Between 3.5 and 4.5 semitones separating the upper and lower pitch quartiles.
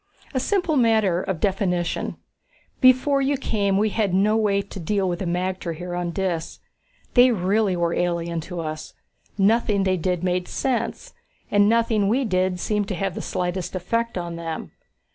Yes: average, 3.8 semitones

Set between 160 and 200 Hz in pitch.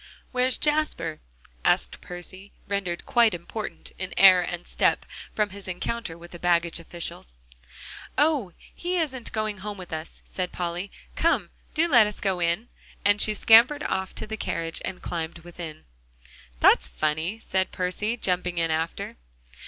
Yes: medium, 185 Hz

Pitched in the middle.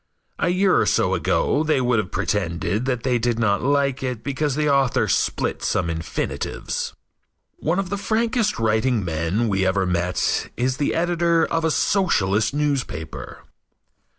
No: low, 125 Hz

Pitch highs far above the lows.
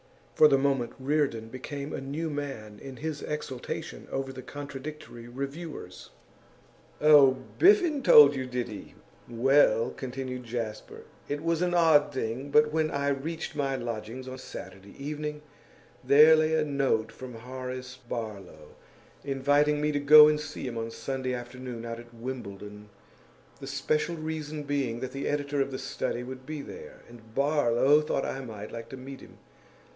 No: average, 3.6 semitones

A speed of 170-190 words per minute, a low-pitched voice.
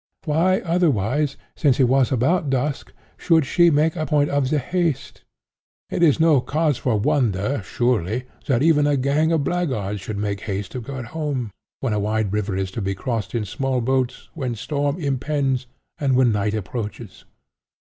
Yes: average, 175 wpm; low, 130 Hz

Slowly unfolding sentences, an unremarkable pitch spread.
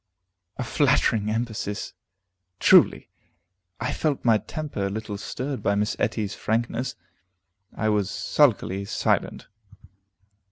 Yes: slow, 110 wpm; average, 3.3 semitones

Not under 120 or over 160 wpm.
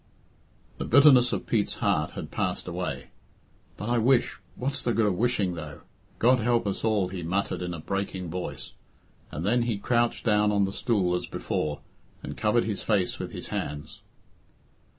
No: average, 175 wpm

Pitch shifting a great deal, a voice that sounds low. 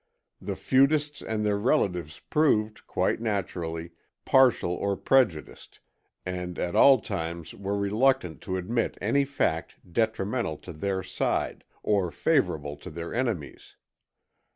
Yes: wide, 5.8 semitones; low, 100 Hz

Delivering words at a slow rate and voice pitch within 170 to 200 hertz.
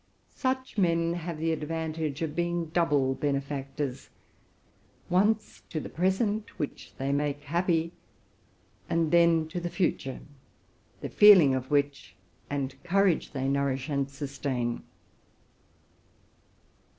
No: slow, 115 wpm; medium, 155 Hz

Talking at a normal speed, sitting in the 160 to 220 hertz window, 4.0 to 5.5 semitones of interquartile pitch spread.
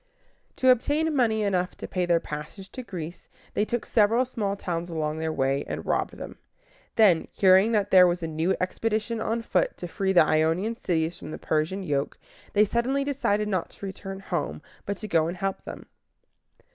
Yes: average, 190 wpm; high, 190 Hz; average, 4.8 semitones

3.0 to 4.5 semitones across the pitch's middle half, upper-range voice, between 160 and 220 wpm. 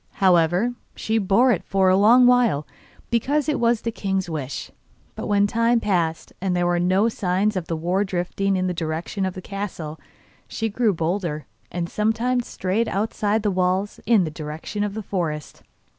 Yes: average, 3.8 semitones; high, 195 Hz; average, 180 wpm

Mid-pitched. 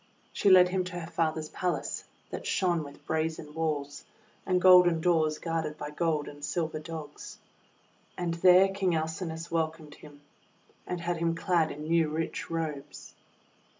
Yes: medium, 165 Hz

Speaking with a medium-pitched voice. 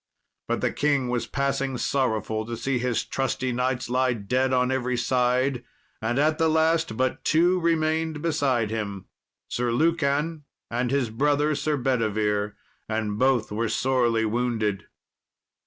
No: low, 125 Hz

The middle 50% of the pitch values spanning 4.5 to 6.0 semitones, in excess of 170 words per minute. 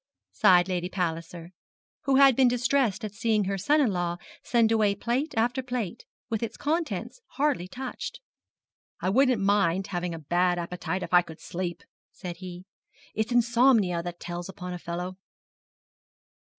No: wide, 5.4 semitones; average, 155 wpm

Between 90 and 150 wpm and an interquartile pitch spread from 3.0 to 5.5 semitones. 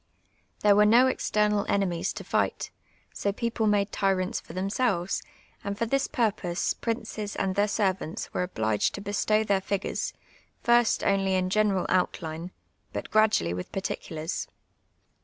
No: average, 140 wpm; narrow, 2.6 semitones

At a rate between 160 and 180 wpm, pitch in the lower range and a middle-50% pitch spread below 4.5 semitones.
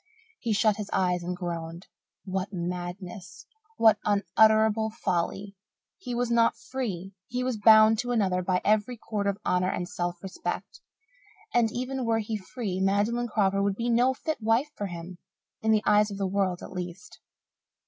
No: average, 170 wpm; high, 205 Hz; average, 3.7 semitones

